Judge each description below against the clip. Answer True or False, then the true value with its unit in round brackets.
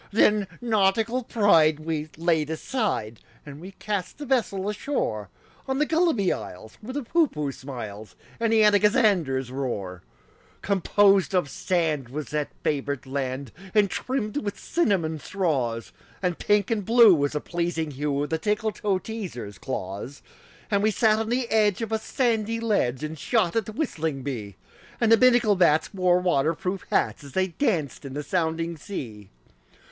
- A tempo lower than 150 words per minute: False (160 wpm)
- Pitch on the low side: False (180 Hz)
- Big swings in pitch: True (7.3 semitones)